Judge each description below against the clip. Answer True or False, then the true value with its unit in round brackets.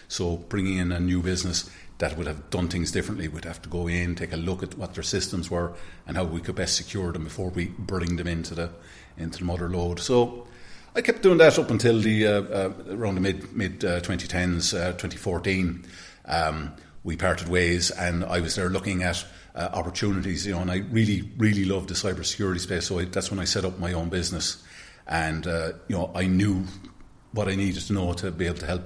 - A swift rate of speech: True (225 wpm)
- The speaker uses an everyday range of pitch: False (1.9 semitones)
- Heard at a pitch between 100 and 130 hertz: False (90 Hz)